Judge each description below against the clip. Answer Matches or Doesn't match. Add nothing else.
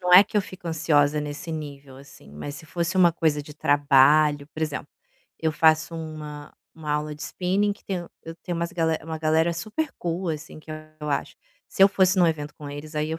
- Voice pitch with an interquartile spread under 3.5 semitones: Matches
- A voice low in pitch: Doesn't match